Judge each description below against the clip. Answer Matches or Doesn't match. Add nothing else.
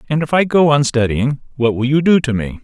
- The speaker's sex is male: Matches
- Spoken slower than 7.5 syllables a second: Matches